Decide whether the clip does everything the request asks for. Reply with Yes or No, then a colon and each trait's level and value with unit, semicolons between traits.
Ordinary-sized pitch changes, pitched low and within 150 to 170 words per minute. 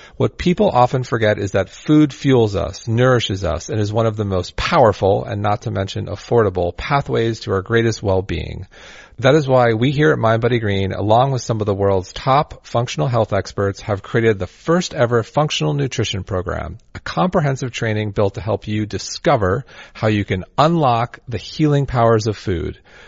No: average, 4.3 semitones; low, 110 Hz; average, 180 wpm